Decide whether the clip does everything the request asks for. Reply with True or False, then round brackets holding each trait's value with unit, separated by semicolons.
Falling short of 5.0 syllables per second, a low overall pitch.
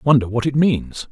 True (4.7 syllables/s; 130 Hz)